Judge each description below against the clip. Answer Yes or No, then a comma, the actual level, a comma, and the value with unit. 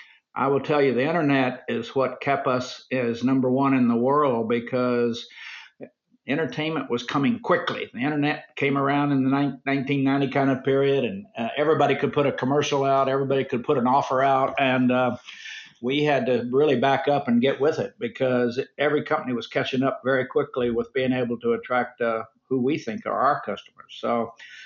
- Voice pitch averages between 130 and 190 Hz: Yes, low, 135 Hz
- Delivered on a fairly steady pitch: Yes, narrow, 2.1 semitones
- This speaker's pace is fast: No, average, 190 wpm